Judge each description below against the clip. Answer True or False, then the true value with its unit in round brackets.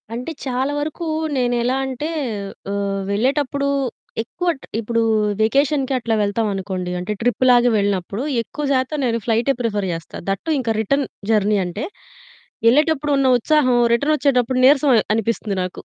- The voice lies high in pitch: True (245 Hz)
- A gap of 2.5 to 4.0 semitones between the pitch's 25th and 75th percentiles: False (4.7 semitones)